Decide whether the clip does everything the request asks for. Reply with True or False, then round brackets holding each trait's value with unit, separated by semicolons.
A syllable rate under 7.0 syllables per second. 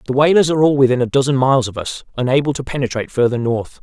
False (7.3 syllables/s)